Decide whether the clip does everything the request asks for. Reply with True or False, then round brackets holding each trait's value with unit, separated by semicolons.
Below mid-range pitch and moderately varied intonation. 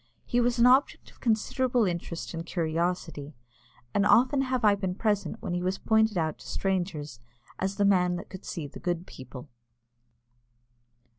False (190 Hz; 4.5 semitones)